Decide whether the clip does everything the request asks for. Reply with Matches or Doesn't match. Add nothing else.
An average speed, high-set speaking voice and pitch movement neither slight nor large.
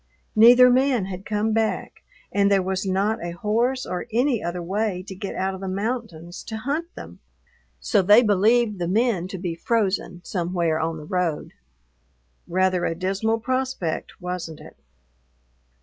Matches